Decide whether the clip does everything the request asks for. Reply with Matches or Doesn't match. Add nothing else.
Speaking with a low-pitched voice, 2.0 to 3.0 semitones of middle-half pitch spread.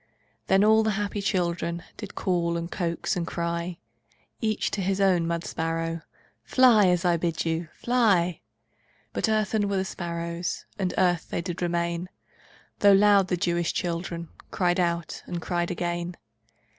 Doesn't match